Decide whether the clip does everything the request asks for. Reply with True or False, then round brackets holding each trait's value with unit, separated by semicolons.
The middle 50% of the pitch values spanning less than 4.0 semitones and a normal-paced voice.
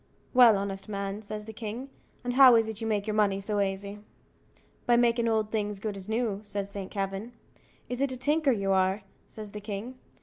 False (2.8 semitones; 210 wpm)